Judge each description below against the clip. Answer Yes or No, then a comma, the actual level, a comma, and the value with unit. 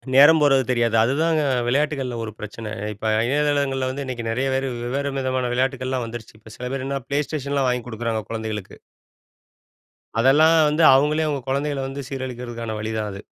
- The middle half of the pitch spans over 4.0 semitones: No, average, 3.3 semitones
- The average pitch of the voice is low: Yes, low, 130 Hz